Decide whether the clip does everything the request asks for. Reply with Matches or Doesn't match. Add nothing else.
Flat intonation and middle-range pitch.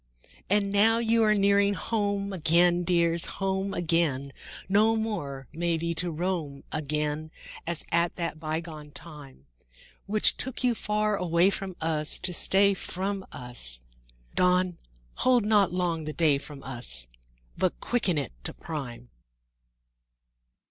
Doesn't match